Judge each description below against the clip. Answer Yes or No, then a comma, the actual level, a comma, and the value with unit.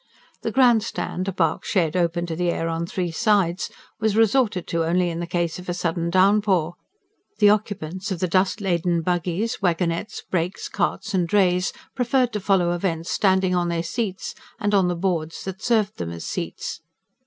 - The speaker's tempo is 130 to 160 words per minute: No, average, 185 wpm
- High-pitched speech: No, medium, 180 Hz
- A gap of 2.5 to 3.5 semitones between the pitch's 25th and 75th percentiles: Yes, average, 3.1 semitones